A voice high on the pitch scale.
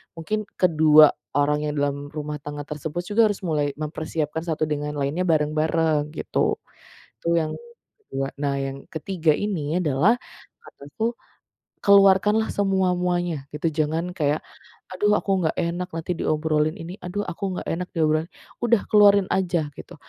No: medium, 160 Hz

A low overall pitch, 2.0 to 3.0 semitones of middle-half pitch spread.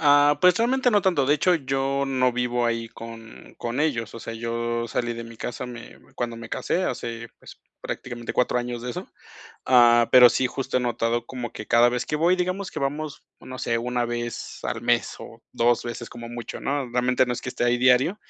Yes: low, 125 Hz; narrow, 2.6 semitones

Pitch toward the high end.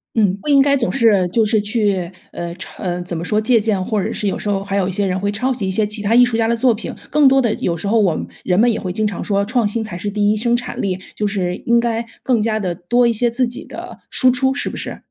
Yes: high, 215 Hz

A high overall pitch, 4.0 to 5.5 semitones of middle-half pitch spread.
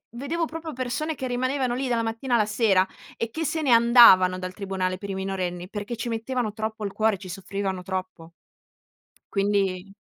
Yes: high, 215 Hz; average, 4.5 semitones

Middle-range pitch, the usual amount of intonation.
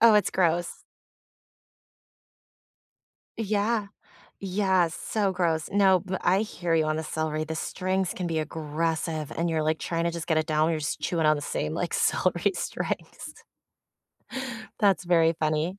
Yes: medium, 165 Hz; average, 3.1 semitones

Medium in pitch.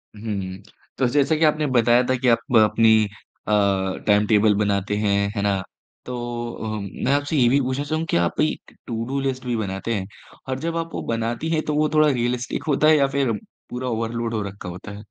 No: low, 115 Hz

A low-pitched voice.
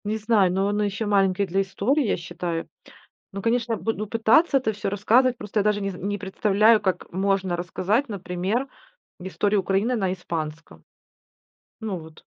No: high, 200 Hz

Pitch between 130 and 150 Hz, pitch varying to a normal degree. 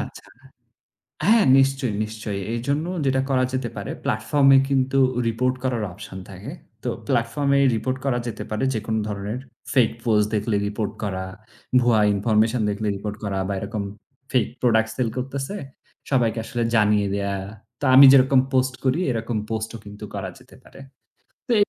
No: low, 115 Hz; average, 3.8 semitones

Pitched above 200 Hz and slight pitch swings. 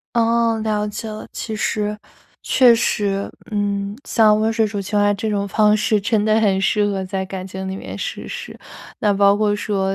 Yes: high, 210 Hz; narrow, 1.6 semitones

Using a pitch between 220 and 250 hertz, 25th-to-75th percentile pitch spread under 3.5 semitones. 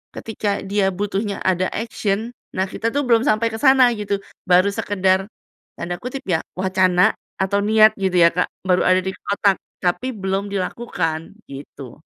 No: high, 195 Hz; average, 2.7 semitones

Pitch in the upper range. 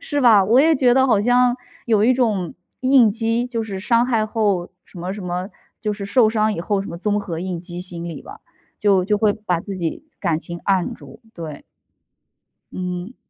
Yes: high, 205 Hz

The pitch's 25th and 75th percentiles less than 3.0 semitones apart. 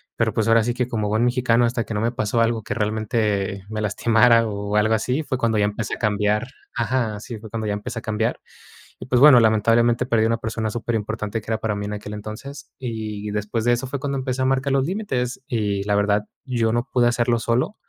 Yes: narrow, 2.5 semitones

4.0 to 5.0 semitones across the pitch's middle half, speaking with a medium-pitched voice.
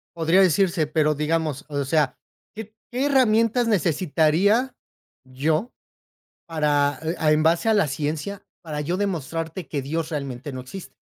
Yes: average, 4.7 semitones; medium, 160 Hz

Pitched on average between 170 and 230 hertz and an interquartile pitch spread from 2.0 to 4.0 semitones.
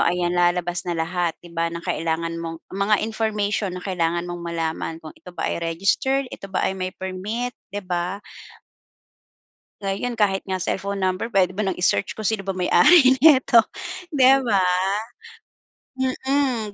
Yes: high, 190 Hz; average, 3.6 semitones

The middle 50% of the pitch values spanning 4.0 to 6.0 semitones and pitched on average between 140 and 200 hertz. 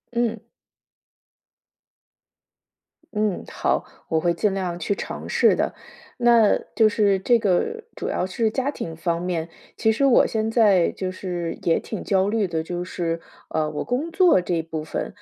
Yes: average, 4.6 semitones; high, 190 Hz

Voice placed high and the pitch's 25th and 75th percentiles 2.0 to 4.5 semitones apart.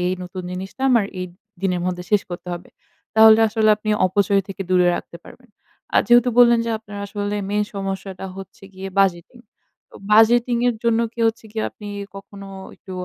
Yes: high, 205 Hz; average, 2.9 semitones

